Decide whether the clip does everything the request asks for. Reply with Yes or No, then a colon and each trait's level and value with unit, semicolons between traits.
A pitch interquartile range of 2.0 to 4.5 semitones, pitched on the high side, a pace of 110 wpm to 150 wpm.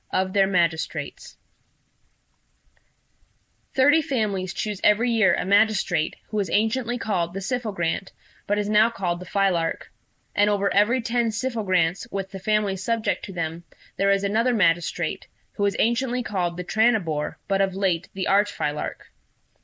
Yes: average, 3.2 semitones; high, 200 Hz; average, 145 wpm